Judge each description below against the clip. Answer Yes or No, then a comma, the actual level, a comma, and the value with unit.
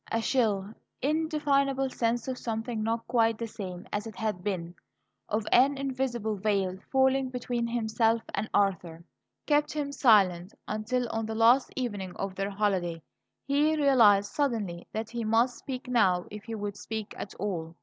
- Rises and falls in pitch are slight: No, average, 4.0 semitones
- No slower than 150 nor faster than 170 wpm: Yes, average, 160 wpm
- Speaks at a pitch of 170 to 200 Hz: No, high, 225 Hz